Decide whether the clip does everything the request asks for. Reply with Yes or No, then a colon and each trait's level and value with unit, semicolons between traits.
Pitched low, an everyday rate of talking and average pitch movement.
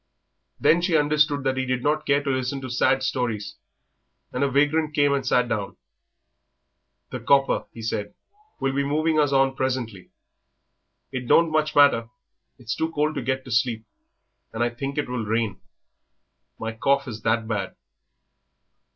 Yes: low, 130 Hz; average, 165 wpm; average, 3.6 semitones